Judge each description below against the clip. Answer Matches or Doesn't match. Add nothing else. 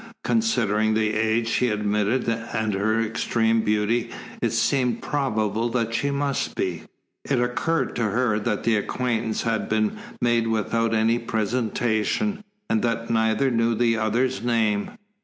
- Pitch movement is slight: Matches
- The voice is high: Doesn't match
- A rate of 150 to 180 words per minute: Doesn't match